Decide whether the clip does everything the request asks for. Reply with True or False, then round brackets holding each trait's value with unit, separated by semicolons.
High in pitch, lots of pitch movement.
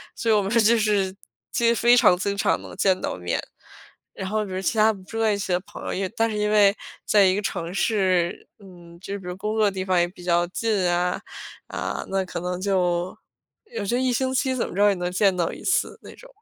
False (195 Hz; 3.1 semitones)